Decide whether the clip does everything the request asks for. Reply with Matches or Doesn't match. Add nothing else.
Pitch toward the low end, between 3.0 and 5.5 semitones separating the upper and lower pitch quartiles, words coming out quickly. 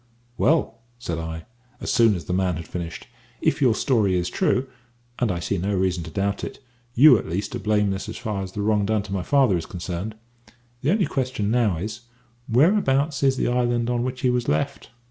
Matches